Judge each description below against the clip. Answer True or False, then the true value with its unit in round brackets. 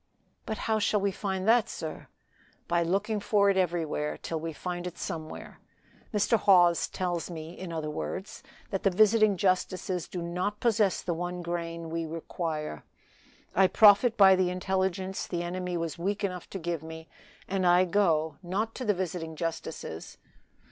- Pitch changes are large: False (2.9 semitones)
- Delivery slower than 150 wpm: False (165 wpm)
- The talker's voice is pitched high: False (180 Hz)